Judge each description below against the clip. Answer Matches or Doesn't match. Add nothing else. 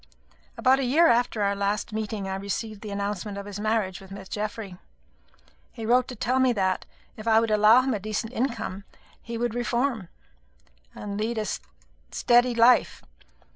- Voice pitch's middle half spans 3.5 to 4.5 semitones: Doesn't match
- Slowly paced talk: Doesn't match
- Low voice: Doesn't match